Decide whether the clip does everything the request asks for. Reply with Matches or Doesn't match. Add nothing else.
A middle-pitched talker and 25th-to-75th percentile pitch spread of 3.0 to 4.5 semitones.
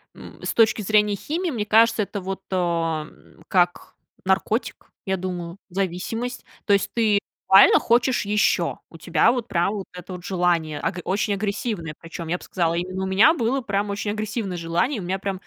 Doesn't match